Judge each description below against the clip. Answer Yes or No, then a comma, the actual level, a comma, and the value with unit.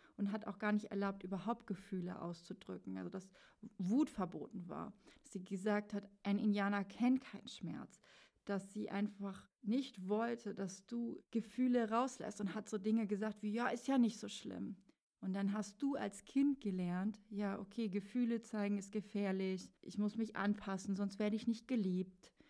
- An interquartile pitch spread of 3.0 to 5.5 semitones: No, narrow, 2.5 semitones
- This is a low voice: No, high, 205 Hz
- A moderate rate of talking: Yes, average, 175 wpm